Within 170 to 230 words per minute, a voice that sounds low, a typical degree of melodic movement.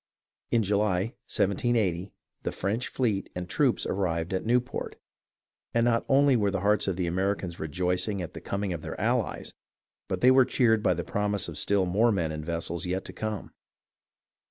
Yes: average, 180 wpm; low, 100 Hz; average, 3.7 semitones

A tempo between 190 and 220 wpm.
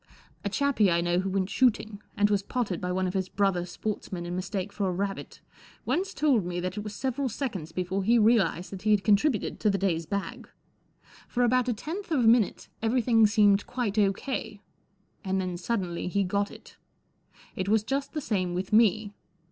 Yes: average, 195 wpm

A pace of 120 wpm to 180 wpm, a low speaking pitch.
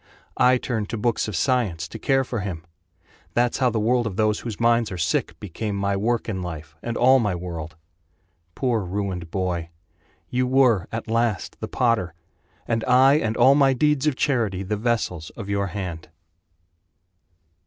Yes: average, 175 wpm; low, 110 Hz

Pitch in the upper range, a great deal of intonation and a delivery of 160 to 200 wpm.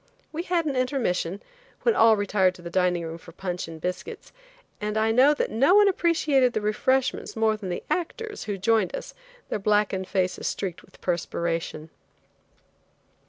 Yes: high, 210 Hz; wide, 6.5 semitones; average, 165 wpm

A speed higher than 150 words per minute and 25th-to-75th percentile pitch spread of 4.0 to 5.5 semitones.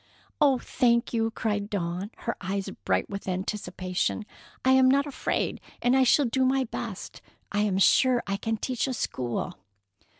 Yes: average, 165 wpm; average, 4.7 semitones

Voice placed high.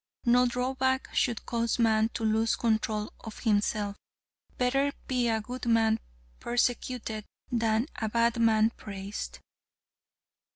Yes: high, 230 Hz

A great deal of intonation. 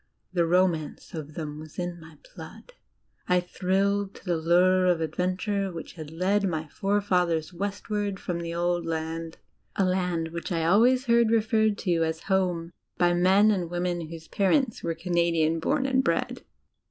No: average, 3.2 semitones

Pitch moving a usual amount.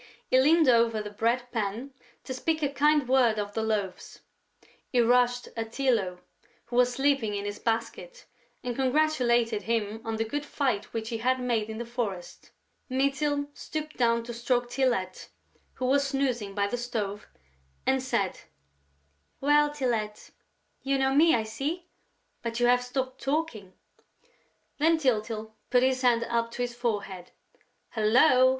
Yes: average, 3.4 semitones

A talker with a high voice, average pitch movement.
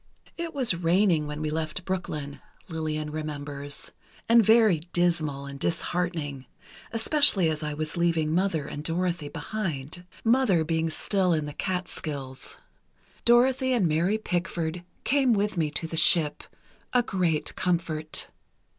No: medium, 165 Hz; average, 3.8 semitones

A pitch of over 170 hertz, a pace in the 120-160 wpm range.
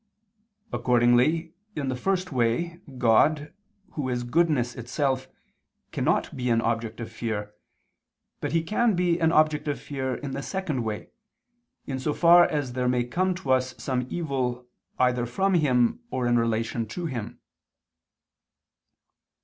No: low, 130 Hz; average, 145 wpm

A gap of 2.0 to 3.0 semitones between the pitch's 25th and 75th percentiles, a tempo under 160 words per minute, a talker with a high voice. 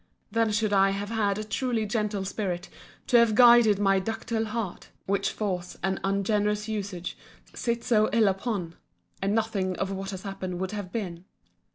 No: narrow, 2.4 semitones; average, 170 wpm; high, 205 Hz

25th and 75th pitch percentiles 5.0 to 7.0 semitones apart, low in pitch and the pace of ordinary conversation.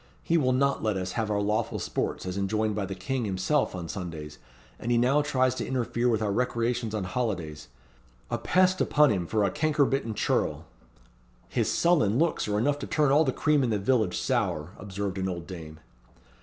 Yes: wide, 5.6 semitones; low, 110 Hz; average, 195 wpm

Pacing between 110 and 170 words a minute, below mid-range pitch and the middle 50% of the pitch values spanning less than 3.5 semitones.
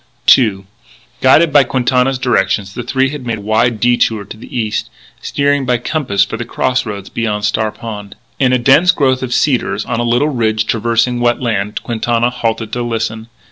No: average, 185 wpm; low, 120 Hz; average, 2.8 semitones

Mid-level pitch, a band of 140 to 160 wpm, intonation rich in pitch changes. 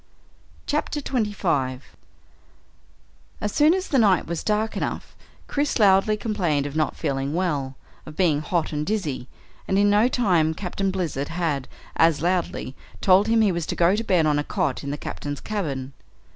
No: medium, 175 Hz; average, 170 wpm; wide, 6.0 semitones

